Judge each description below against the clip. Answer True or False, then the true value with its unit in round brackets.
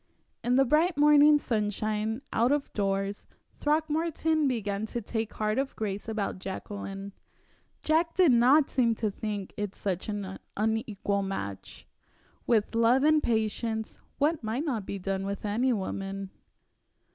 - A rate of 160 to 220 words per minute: False (140 wpm)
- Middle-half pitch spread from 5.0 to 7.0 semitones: True (5.3 semitones)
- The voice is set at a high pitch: True (220 Hz)